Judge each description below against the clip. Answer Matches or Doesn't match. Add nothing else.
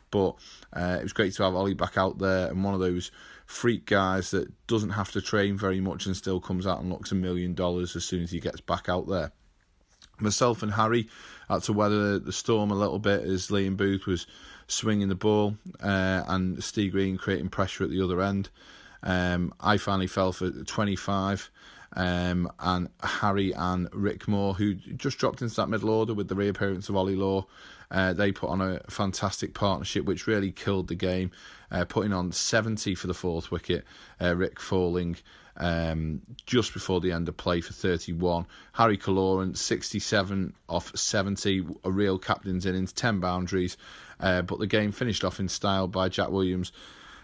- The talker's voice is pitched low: Matches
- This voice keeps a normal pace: Matches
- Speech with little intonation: Matches